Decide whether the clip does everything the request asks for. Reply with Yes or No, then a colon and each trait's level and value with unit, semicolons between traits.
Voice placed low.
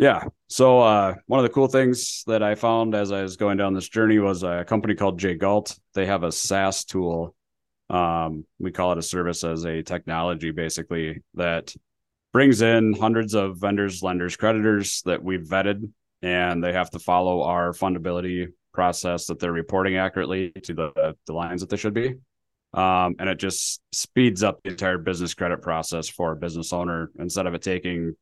Yes: very low, 90 Hz